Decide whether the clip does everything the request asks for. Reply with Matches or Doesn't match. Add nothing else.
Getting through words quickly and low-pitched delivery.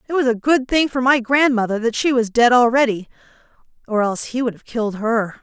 Doesn't match